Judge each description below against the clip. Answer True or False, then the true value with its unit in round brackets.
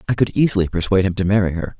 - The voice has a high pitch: False (100 Hz)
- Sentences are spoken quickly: True (270 wpm)